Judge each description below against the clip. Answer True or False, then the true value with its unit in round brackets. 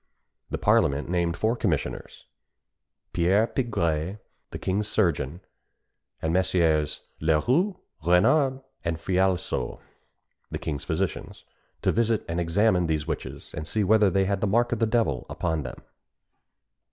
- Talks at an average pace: False (130 wpm)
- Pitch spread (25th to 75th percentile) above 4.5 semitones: True (5.2 semitones)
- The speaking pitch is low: True (90 Hz)